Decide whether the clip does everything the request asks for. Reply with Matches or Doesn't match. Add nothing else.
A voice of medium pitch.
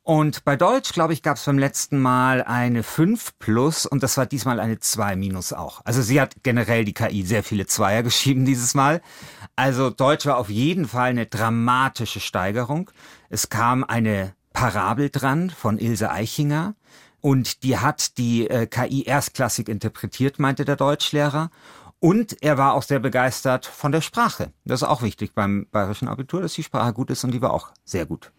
Doesn't match